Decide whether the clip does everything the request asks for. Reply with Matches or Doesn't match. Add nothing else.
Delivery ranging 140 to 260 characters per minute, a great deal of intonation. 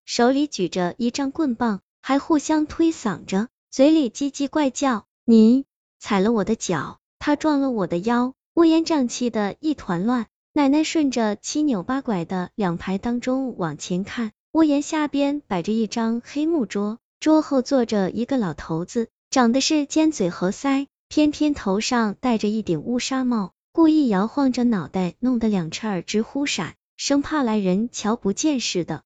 Matches